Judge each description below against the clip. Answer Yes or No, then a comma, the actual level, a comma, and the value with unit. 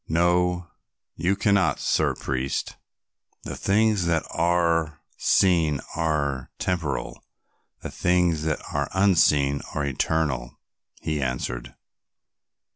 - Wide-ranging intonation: No, average, 3.8 semitones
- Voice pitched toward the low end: Yes, very low, 80 Hz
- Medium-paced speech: No, slow, 100 wpm